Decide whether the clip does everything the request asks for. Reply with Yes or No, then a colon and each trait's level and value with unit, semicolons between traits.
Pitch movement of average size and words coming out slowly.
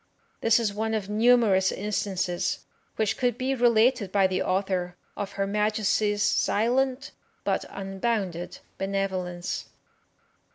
Yes: average, 3.0 semitones; slow, 115 wpm